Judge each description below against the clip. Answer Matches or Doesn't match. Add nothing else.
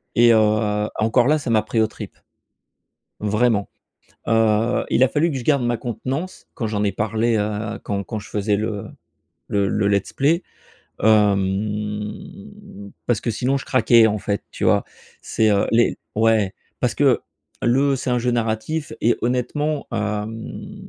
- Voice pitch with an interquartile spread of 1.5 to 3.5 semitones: Matches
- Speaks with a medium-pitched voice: Doesn't match